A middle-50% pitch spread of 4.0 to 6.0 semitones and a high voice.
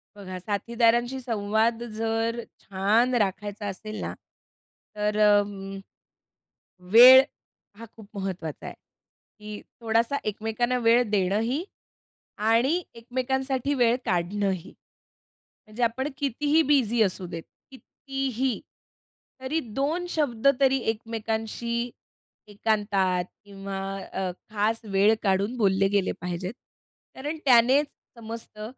No: average, 3.5 semitones; high, 225 Hz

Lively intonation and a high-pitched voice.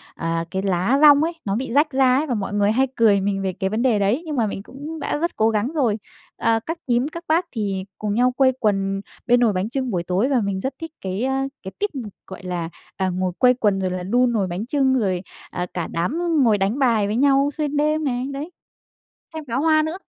Yes: wide, 6.0 semitones; high, 235 Hz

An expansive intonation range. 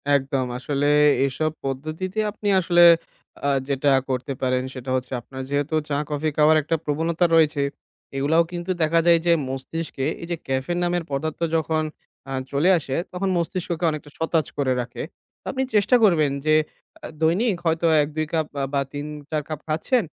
No: average, 3.3 semitones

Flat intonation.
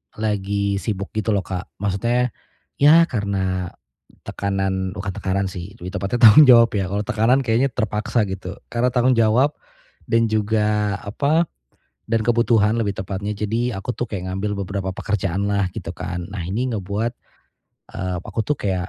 No: average, 3.0 semitones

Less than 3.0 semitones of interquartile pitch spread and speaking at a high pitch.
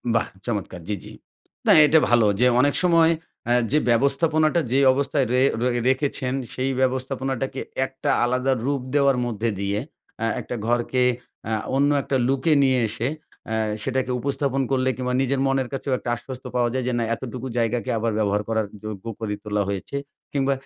No: narrow, 2.5 semitones; low, 130 Hz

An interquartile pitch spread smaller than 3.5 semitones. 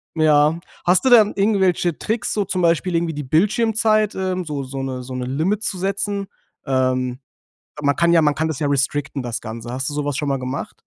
No: wide, 6.0 semitones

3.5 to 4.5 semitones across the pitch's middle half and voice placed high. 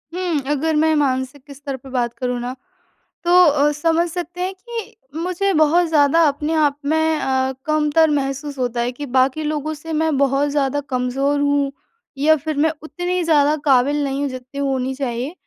No: average, 2.8 semitones; very high, 290 Hz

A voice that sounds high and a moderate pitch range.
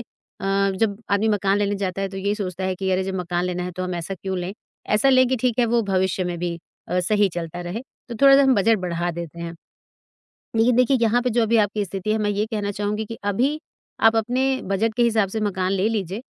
Yes: high, 200 Hz; average, 3.4 semitones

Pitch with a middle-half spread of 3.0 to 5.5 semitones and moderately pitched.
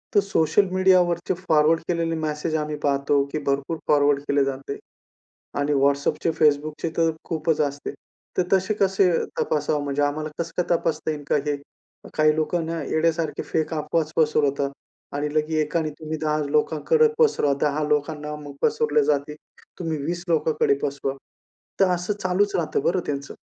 No: narrow, 2.4 semitones; medium, 155 Hz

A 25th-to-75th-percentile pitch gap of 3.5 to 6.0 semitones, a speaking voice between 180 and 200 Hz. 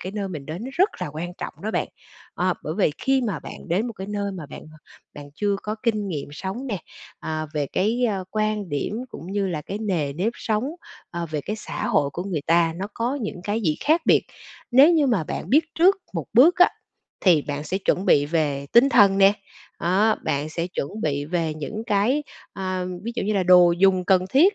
Yes: average, 5.0 semitones; high, 195 Hz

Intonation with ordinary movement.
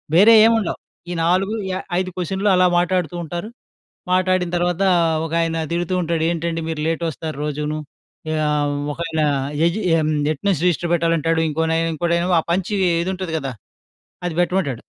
No: narrow, 2.3 semitones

